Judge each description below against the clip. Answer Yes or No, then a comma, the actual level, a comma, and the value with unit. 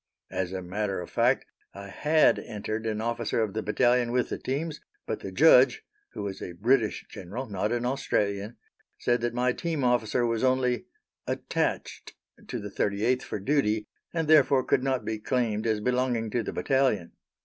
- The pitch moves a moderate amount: Yes, average, 3.5 semitones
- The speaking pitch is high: No, low, 120 Hz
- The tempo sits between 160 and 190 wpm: Yes, average, 175 wpm